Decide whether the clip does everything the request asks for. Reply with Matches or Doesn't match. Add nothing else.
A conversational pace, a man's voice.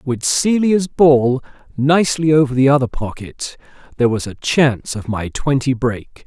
Matches